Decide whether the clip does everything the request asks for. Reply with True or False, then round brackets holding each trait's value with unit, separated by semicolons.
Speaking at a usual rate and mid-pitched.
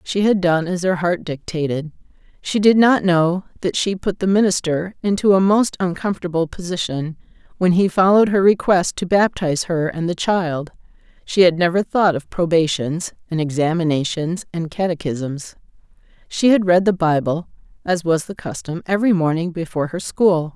True (165 wpm; 175 Hz)